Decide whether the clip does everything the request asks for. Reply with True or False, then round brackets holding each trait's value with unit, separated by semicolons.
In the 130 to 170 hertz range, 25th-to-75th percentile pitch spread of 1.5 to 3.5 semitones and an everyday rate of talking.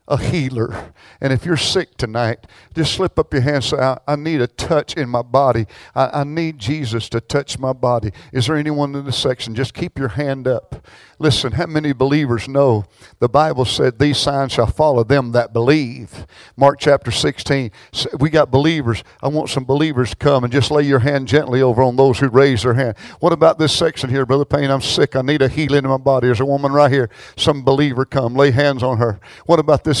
False (135 Hz; 2.8 semitones; 225 wpm)